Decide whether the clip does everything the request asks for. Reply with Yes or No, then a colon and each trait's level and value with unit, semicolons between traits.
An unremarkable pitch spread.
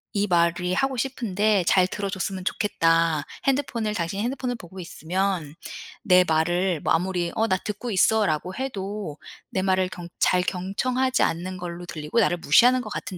Yes: average, 3.5 semitones